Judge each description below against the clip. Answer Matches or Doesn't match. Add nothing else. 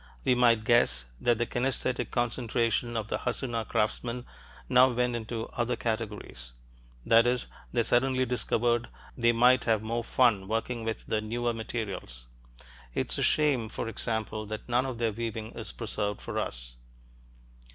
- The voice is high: Doesn't match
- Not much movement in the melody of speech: Matches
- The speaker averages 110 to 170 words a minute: Matches